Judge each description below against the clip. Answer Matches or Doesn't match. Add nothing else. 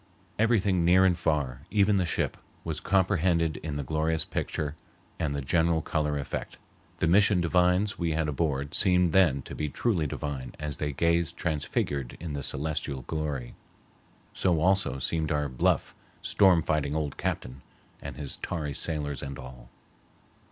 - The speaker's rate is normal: Matches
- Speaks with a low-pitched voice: Matches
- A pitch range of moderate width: Matches